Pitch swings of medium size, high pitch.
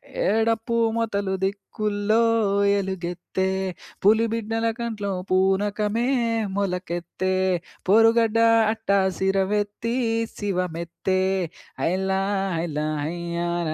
Yes: average, 3.0 semitones; high, 195 Hz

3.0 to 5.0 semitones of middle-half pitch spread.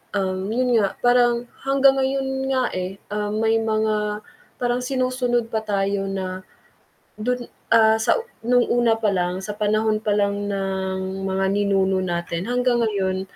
Yes: average, 3.9 semitones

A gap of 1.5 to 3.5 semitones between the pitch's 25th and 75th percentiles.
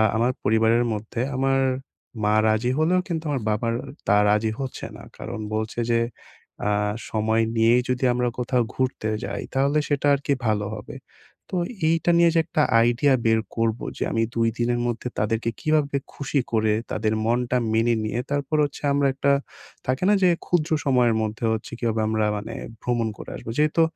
No: average, 3.9 semitones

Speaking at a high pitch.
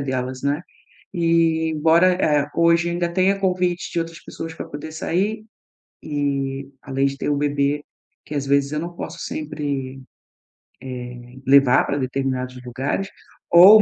No: medium, 145 Hz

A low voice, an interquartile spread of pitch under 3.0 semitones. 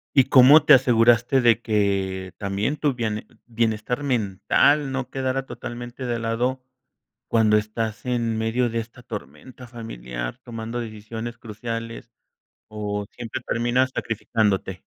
Yes: low, 115 Hz; narrow, 2.5 semitones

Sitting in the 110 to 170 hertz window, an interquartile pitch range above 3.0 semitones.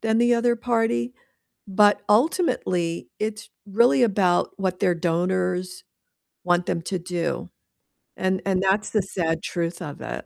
No: medium, 185 Hz; average, 3.7 semitones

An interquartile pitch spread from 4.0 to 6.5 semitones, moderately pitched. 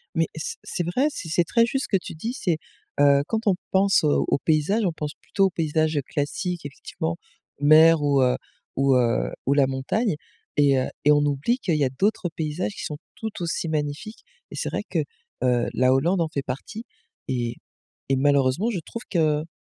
Yes: average, 4.6 semitones; medium, 155 Hz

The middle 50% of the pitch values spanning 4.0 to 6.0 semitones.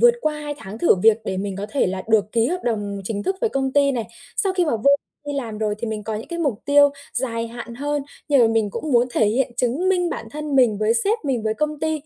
Yes: average, 5.2 semitones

